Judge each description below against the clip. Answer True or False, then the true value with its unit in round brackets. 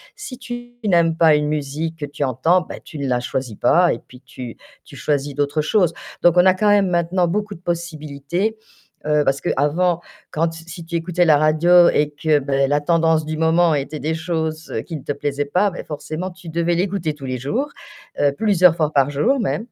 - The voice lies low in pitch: False (160 Hz)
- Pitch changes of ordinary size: True (3.3 semitones)